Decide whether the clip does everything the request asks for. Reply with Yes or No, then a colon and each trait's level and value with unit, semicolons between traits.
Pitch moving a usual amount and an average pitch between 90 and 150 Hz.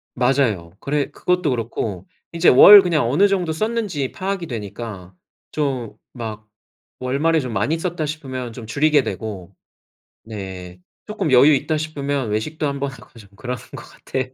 No: wide, 5.8 semitones; low, 135 Hz